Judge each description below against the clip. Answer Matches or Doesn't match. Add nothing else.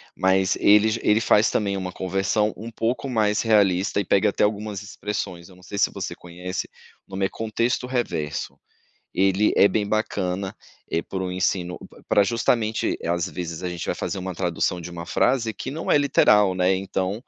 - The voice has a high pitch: Doesn't match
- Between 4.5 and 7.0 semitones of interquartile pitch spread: Doesn't match